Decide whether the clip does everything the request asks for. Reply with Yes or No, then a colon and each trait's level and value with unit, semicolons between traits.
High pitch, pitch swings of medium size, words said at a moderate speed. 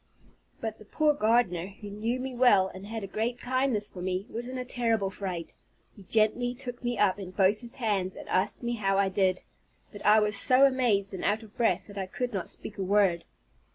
No: high, 210 Hz; average, 3.8 semitones; fast, 225 wpm